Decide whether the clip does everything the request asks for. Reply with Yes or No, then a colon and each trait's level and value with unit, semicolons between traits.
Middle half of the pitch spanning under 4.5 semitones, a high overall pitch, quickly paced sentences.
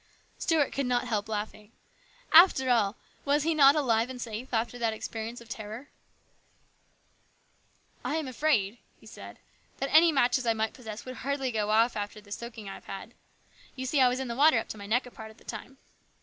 Yes: average, 3.5 semitones; high, 240 Hz; fast, 210 wpm